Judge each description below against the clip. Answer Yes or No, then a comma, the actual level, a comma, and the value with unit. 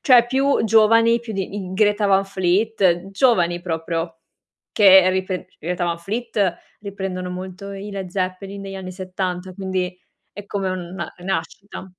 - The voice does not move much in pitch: Yes, narrow, 2.0 semitones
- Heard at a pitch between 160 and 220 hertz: Yes, high, 190 Hz